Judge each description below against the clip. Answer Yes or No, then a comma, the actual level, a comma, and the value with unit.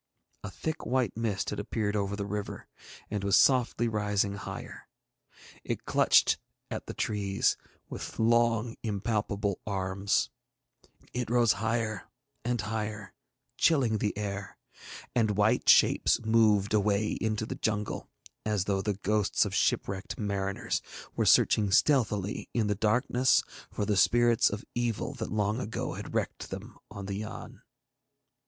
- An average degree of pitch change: No, narrow, 2.2 semitones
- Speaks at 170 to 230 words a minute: No, average, 140 wpm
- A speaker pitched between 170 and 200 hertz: No, low, 105 Hz